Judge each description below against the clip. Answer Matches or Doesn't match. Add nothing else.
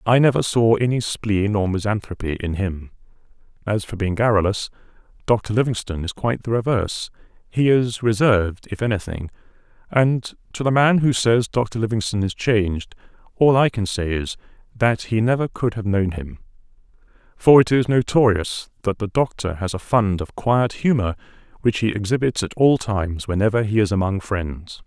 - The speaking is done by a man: Matches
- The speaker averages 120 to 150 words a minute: Doesn't match